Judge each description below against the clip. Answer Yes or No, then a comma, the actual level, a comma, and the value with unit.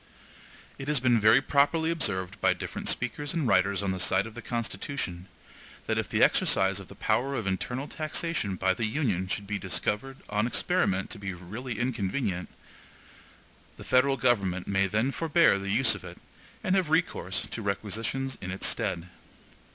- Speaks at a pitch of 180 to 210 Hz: No, low, 110 Hz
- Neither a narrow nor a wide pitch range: No, wide, 5.9 semitones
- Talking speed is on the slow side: No, average, 175 wpm